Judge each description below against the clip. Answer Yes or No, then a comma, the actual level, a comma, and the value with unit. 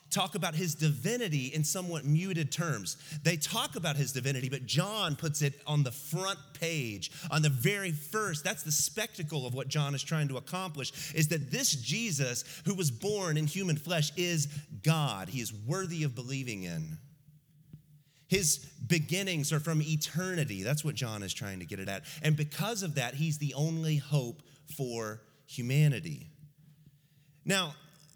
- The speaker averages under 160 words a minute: No, average, 165 wpm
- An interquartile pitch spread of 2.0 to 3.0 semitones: Yes, narrow, 2.4 semitones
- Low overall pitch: No, medium, 150 Hz